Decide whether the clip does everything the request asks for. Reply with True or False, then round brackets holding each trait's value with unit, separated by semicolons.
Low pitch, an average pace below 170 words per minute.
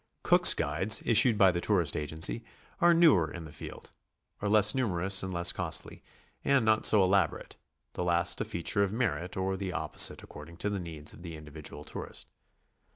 False (95 Hz; 185 wpm)